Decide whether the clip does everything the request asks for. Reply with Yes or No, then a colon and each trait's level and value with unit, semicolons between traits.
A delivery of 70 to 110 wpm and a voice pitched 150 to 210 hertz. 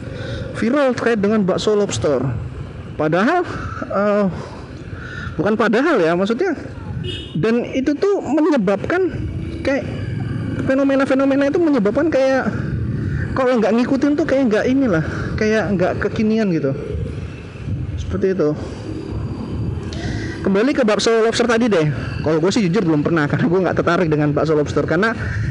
No: average, 125 wpm; medium, 185 Hz